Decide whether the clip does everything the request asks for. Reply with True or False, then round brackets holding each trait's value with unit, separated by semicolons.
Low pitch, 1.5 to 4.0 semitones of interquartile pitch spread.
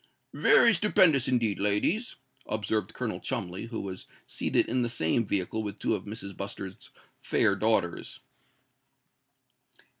True (110 Hz; 3.7 semitones)